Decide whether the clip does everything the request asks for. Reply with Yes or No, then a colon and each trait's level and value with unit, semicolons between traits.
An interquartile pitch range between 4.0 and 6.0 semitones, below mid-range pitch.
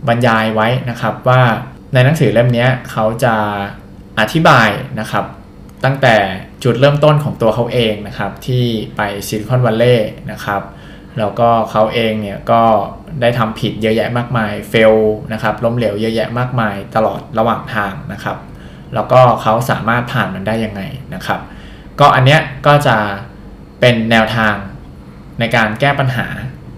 No: average, 2.8 semitones; low, 110 Hz